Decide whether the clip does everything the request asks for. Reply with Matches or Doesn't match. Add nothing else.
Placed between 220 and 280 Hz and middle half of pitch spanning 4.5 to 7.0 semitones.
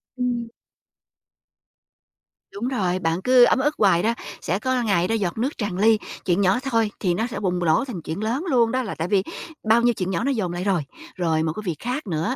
Doesn't match